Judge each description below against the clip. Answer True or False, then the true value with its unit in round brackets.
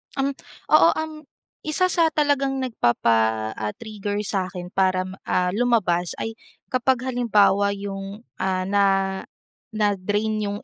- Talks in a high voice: True (205 Hz)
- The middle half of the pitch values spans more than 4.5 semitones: True (4.9 semitones)